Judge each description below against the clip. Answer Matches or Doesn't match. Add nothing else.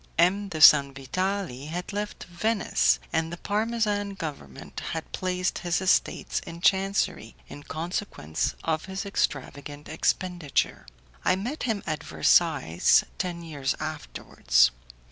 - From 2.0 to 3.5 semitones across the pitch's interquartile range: Doesn't match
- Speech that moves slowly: Matches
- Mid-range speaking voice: Matches